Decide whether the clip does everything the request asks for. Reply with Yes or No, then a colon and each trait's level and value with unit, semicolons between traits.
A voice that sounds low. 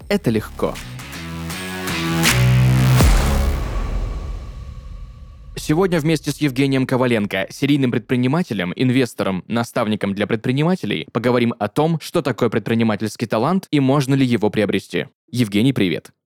Yes: low, 115 Hz